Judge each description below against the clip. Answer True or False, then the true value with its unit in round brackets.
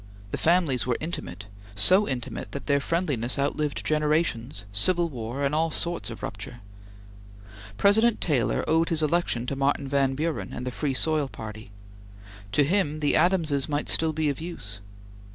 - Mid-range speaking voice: True (145 Hz)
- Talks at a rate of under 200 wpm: True (160 wpm)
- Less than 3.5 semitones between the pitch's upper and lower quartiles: False (4.5 semitones)